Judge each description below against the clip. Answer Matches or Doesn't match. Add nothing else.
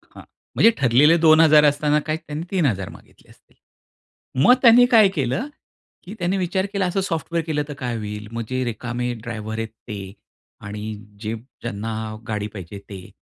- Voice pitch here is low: Matches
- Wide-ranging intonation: Matches